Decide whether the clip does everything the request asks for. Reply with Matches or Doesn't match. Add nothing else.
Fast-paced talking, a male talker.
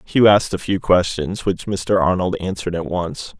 Doesn't match